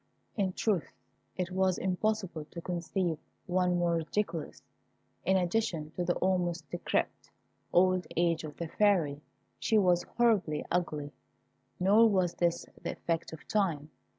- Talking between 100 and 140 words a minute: Yes, slow, 135 wpm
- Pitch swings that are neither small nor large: No, narrow, 2.3 semitones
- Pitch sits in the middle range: Yes, medium, 175 Hz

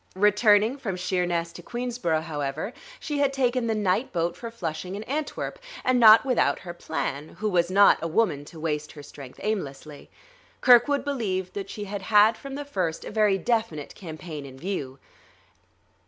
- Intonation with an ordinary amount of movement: No, wide, 6.2 semitones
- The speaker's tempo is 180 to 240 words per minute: No, average, 170 wpm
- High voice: Yes, high, 195 Hz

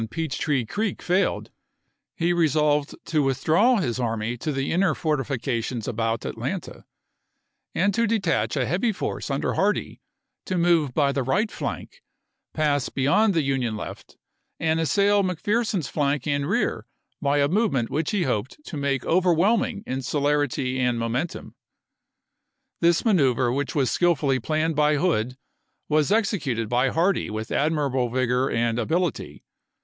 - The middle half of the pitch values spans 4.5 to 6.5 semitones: Yes, average, 5.2 semitones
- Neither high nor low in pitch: Yes, medium, 145 Hz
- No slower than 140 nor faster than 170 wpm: Yes, average, 145 wpm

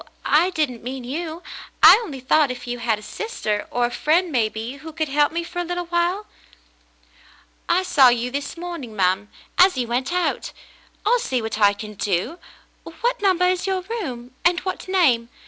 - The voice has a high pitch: Yes, very high, 290 Hz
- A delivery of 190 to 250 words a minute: Yes, average, 195 wpm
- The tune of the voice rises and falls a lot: Yes, wide, 6.8 semitones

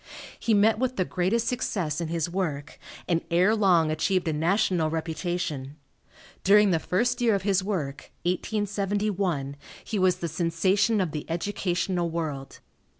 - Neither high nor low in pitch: Yes, medium, 180 Hz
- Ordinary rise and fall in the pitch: Yes, average, 3.9 semitones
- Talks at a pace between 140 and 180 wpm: Yes, average, 150 wpm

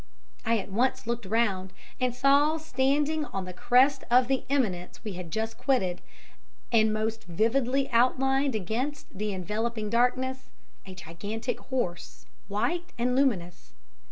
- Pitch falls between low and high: No, high, 235 Hz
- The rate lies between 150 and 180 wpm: No, slow, 135 wpm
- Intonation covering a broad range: No, average, 4.5 semitones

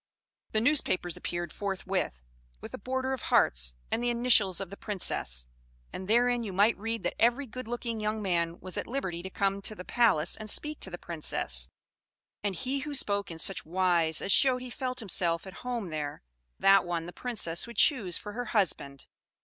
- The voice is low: No, high, 200 Hz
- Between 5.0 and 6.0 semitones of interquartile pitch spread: Yes, wide, 5.6 semitones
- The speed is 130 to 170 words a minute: No, average, 195 wpm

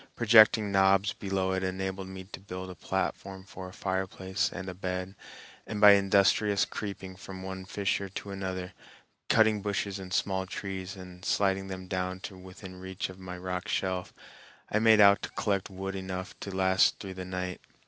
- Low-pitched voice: Yes, very low, 95 Hz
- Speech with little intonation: Yes, narrow, 1.0 semitones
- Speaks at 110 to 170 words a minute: No, average, 180 wpm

